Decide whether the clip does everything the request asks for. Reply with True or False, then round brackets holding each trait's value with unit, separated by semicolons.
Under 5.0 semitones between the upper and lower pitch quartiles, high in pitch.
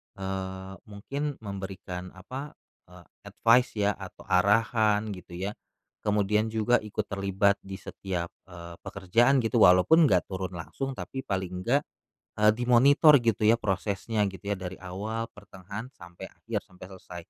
False (3.4 semitones; 100 Hz)